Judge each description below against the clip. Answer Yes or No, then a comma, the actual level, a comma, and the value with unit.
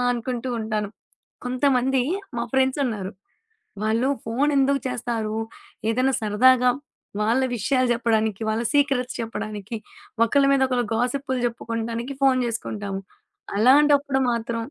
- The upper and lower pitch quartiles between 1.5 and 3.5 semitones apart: Yes, average, 2.9 semitones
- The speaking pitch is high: Yes, high, 240 Hz